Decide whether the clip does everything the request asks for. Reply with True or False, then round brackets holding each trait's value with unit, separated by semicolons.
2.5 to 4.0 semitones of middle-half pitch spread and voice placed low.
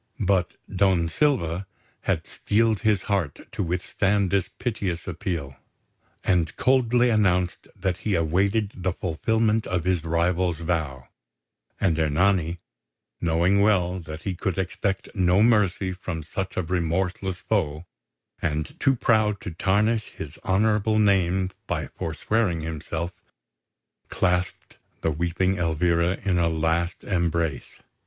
True (3.1 semitones; 90 Hz)